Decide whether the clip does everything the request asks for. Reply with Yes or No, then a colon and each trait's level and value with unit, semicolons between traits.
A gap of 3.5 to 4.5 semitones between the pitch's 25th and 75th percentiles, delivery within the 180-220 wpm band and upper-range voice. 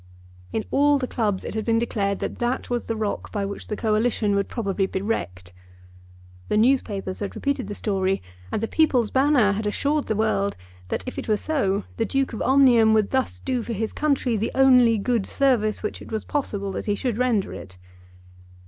Yes: average, 3.9 semitones; average, 200 wpm; high, 220 Hz